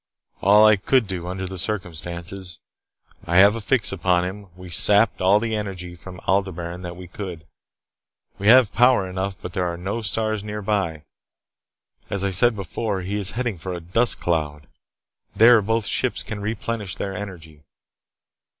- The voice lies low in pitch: Yes, very low, 95 Hz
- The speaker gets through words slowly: No, average, 170 wpm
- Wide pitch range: No, average, 3.0 semitones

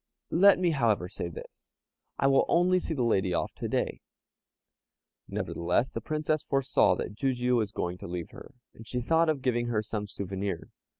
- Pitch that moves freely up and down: Yes, wide, 7.1 semitones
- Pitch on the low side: Yes, low, 120 Hz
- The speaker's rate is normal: Yes, average, 180 wpm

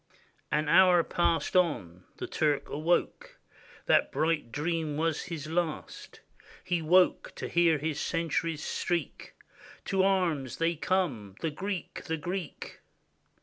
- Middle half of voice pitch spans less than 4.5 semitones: Yes, average, 2.8 semitones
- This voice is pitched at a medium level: Yes, medium, 165 Hz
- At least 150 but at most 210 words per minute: No, slow, 135 wpm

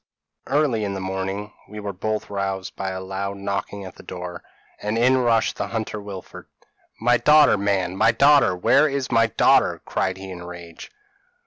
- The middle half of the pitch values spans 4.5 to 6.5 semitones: No, average, 3.3 semitones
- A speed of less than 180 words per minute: No, average, 190 wpm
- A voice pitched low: Yes, low, 100 Hz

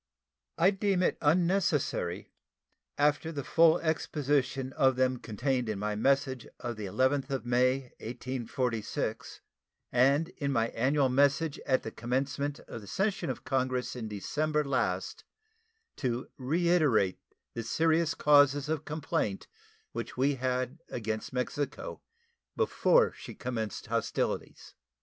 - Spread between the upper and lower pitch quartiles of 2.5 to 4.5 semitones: Yes, average, 3.4 semitones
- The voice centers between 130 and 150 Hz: Yes, low, 135 Hz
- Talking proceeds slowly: Yes, slow, 125 wpm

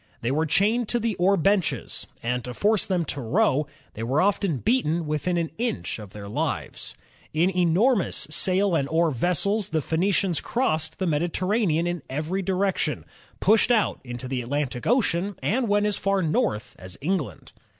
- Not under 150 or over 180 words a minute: Yes, average, 175 wpm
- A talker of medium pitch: Yes, medium, 175 Hz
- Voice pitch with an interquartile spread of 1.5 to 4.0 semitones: No, average, 5.3 semitones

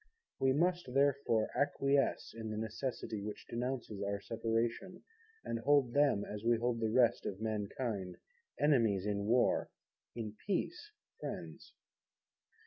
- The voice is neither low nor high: No, low, 115 Hz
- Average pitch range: Yes, average, 4.2 semitones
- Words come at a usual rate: No, slow, 130 wpm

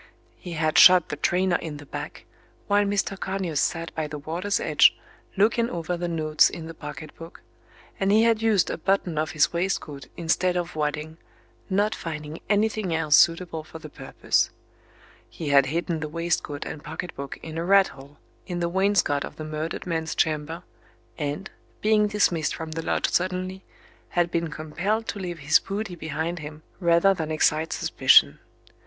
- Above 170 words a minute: Yes, average, 180 wpm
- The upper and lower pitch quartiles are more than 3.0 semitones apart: Yes, average, 3.4 semitones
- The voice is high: No, medium, 165 Hz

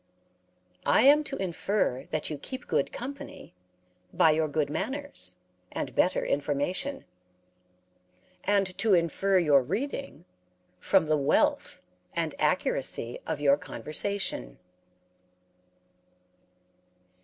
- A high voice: No, medium, 165 Hz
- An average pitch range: No, wide, 6.0 semitones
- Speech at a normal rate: No, slow, 100 wpm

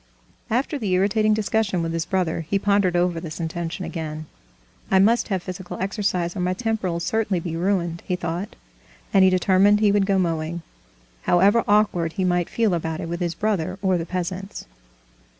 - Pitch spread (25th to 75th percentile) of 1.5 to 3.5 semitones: Yes, average, 2.9 semitones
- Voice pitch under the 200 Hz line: Yes, medium, 185 Hz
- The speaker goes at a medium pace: Yes, average, 180 wpm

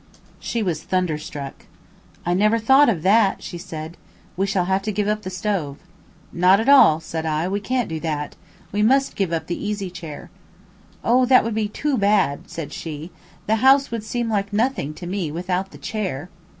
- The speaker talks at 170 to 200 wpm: Yes, average, 190 wpm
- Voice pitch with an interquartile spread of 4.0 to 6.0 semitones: Yes, average, 4.8 semitones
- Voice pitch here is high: Yes, high, 195 Hz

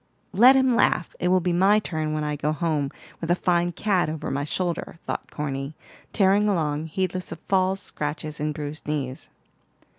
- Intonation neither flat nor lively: Yes, average, 3.7 semitones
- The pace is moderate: Yes, average, 180 wpm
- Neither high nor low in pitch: Yes, medium, 165 Hz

